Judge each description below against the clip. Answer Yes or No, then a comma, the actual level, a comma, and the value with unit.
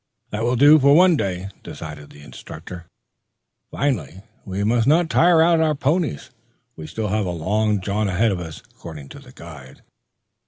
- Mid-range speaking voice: No, low, 105 Hz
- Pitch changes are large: Yes, wide, 8.3 semitones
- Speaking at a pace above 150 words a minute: Yes, average, 180 wpm